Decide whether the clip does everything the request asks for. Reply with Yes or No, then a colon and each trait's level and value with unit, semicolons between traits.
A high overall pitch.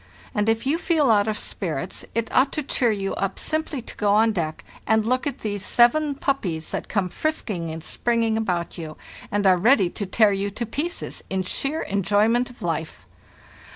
Yes: high, 215 Hz